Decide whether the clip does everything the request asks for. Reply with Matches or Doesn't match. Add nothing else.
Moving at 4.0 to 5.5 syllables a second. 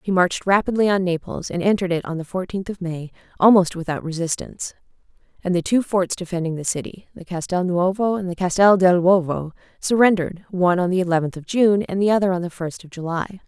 Doesn't match